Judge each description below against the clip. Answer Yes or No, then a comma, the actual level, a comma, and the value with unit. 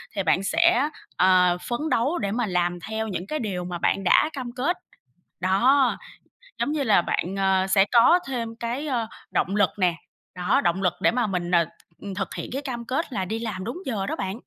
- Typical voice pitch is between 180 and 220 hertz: Yes, high, 215 Hz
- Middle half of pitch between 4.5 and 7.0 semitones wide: Yes, average, 5.1 semitones